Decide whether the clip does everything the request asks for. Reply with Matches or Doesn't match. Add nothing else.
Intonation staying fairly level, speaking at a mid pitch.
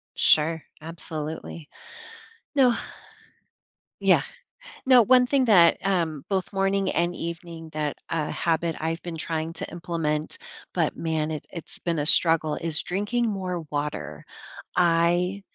Doesn't match